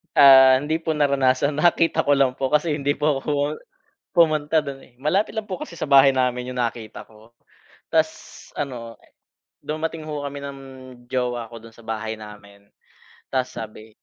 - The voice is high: No, low, 135 Hz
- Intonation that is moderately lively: Yes, average, 3.9 semitones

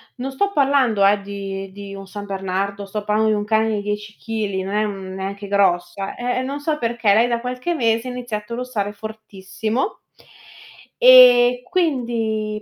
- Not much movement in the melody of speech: No, average, 3.7 semitones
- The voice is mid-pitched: No, high, 215 Hz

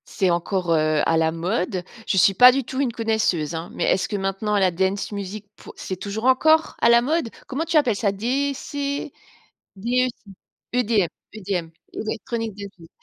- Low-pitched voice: No, high, 210 Hz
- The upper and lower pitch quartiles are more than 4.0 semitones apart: Yes, average, 5.0 semitones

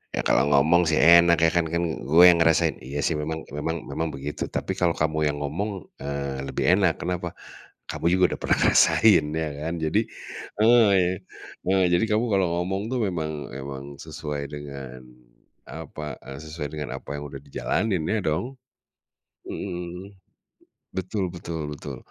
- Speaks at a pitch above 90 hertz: No, very low, 85 Hz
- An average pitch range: Yes, average, 3.6 semitones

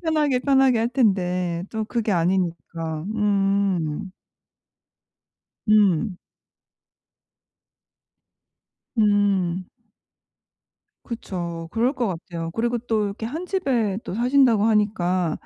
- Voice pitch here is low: No, high, 205 Hz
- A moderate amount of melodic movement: Yes, average, 4.7 semitones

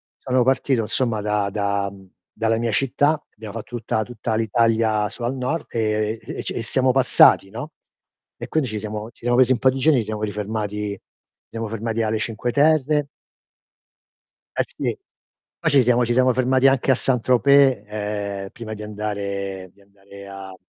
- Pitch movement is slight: No, average, 3.5 semitones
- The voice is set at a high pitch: No, low, 115 Hz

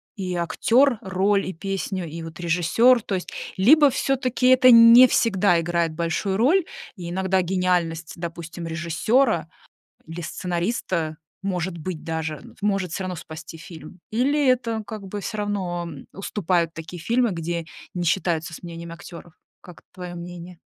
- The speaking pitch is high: No, medium, 180 Hz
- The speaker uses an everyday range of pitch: Yes, average, 3.8 semitones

